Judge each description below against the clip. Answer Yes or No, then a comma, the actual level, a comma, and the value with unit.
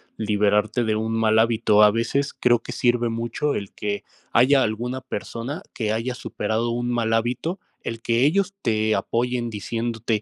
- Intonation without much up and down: Yes, narrow, 2.0 semitones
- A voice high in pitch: No, low, 115 Hz